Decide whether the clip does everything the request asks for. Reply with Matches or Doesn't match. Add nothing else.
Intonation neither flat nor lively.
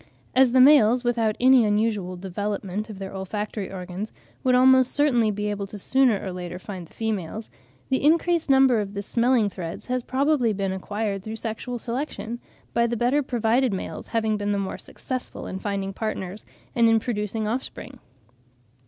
Matches